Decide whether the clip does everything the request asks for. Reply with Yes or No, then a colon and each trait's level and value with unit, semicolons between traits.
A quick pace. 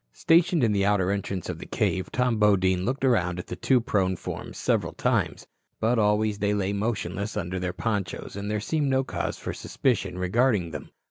No: average, 195 wpm